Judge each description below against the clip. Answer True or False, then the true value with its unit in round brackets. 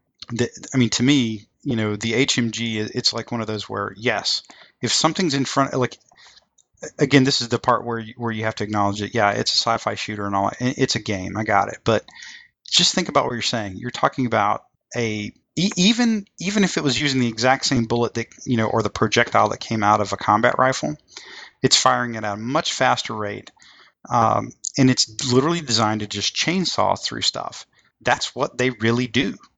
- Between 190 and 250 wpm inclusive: True (205 wpm)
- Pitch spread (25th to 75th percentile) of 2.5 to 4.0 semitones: True (3.4 semitones)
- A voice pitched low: True (120 Hz)